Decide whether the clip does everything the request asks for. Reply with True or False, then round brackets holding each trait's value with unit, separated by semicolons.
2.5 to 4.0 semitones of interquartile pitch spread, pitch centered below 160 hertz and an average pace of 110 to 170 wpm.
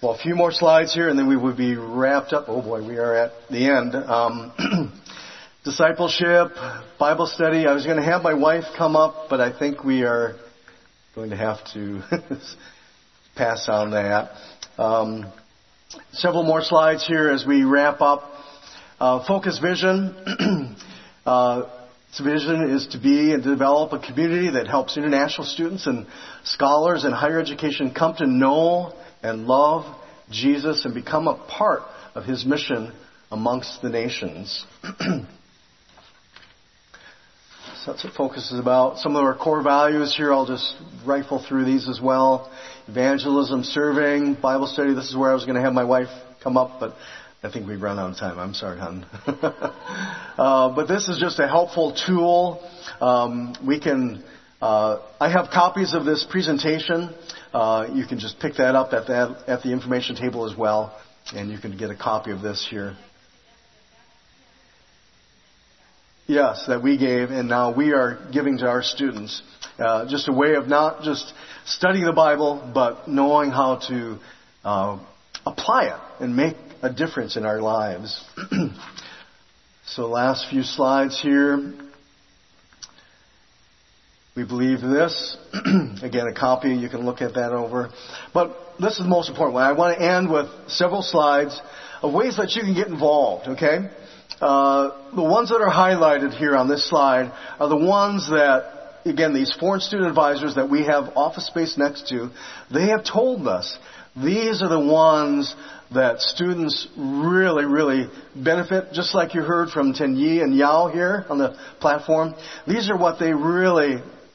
False (4.4 semitones; 140 Hz; 165 wpm)